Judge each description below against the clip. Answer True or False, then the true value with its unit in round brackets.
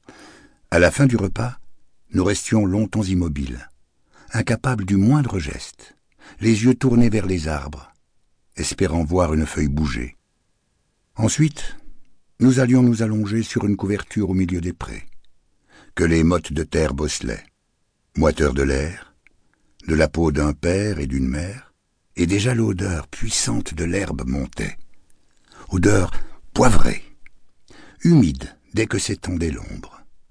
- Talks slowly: True (135 wpm)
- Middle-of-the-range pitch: False (90 Hz)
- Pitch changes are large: True (6.1 semitones)